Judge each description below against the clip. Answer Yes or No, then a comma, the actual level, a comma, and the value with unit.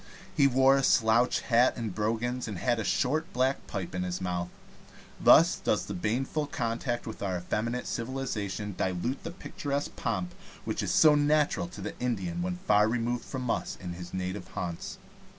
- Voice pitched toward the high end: No, low, 115 Hz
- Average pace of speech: Yes, average, 175 wpm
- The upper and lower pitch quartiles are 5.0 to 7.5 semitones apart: Yes, wide, 5.5 semitones